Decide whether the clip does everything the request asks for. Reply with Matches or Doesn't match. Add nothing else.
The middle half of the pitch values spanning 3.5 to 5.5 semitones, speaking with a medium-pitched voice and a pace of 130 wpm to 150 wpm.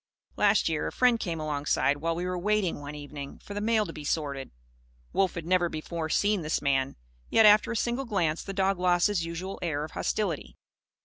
Doesn't match